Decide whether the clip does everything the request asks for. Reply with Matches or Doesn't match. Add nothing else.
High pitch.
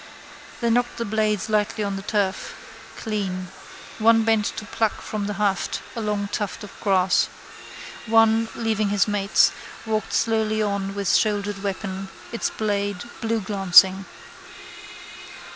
Matches